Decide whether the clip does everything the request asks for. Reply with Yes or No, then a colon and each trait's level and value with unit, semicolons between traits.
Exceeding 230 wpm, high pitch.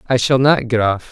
No: fast, 270 wpm; low, 120 Hz